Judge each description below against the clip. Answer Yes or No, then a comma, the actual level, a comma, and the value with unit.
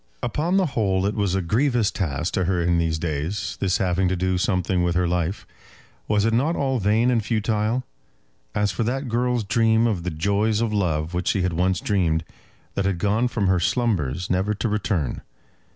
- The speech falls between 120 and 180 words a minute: No, average, 200 wpm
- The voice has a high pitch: No, low, 100 Hz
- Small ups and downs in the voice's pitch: No, average, 4.1 semitones